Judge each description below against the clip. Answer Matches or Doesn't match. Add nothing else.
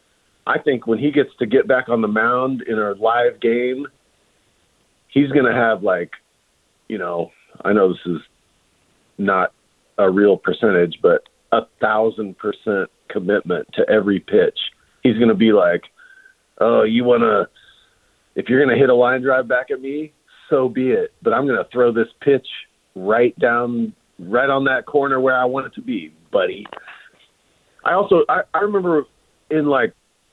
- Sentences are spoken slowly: Doesn't match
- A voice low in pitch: Matches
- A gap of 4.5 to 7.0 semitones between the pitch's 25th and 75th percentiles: Matches